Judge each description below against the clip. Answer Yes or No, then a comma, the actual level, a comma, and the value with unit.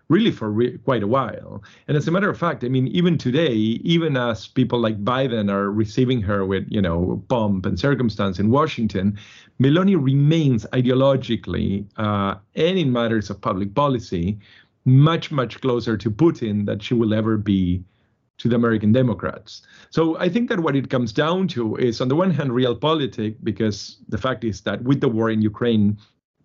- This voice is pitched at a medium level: No, low, 120 Hz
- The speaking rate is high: No, average, 185 wpm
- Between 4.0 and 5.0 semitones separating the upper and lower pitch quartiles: Yes, average, 4.4 semitones